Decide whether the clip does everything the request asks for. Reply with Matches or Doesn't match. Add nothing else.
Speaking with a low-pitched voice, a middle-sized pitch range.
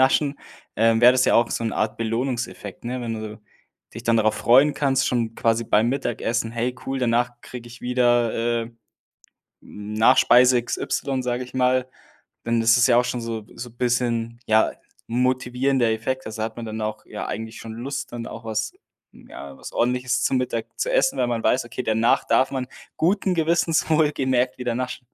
Doesn't match